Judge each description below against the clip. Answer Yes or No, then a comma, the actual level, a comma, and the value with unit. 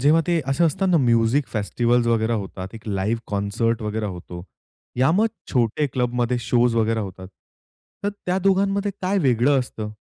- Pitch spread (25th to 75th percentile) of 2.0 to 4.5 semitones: No, average, 4.9 semitones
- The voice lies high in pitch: No, low, 120 Hz